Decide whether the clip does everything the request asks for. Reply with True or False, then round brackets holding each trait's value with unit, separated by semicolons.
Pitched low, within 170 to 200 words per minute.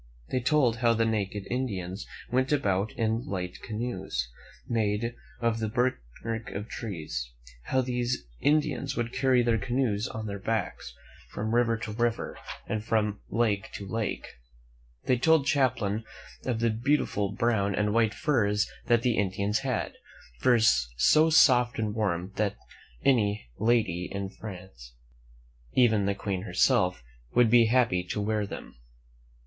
False (110 Hz; 145 wpm)